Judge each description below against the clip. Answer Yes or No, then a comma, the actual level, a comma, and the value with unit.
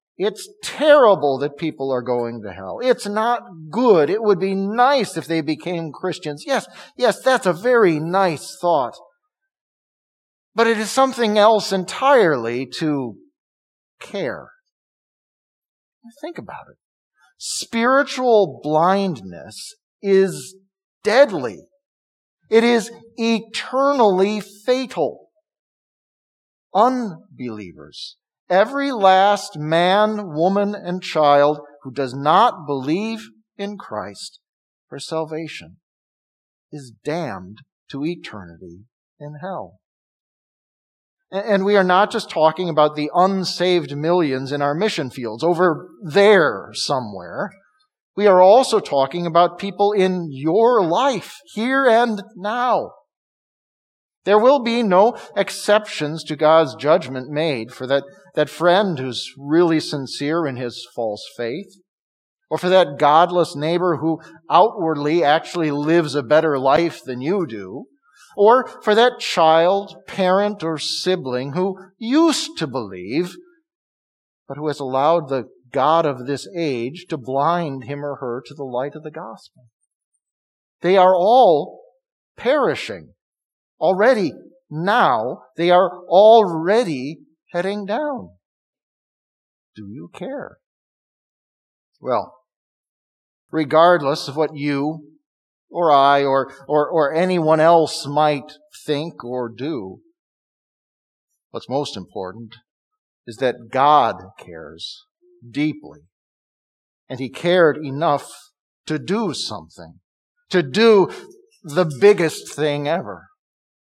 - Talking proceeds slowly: Yes, slow, 110 wpm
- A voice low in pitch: No, medium, 170 Hz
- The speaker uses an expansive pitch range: Yes, wide, 6.5 semitones